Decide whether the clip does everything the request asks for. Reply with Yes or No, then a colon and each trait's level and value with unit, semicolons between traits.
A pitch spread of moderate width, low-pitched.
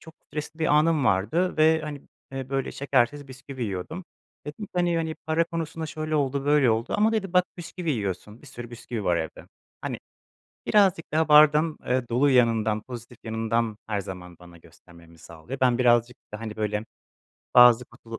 No: wide, 5.9 semitones; low, 130 Hz